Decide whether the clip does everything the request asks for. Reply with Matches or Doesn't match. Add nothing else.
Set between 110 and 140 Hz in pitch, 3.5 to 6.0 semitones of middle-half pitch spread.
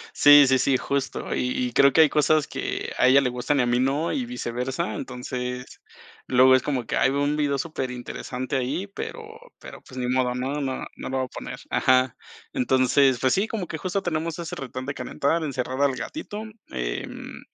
Doesn't match